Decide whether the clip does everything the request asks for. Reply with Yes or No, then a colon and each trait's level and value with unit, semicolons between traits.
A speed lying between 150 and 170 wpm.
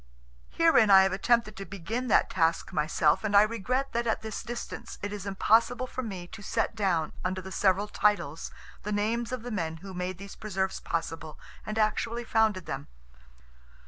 No: average, 180 wpm